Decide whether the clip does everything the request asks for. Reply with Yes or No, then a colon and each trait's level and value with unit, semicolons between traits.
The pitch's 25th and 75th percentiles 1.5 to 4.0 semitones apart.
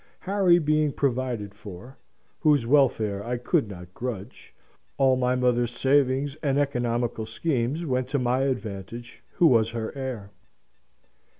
Yes: average, 3.3 semitones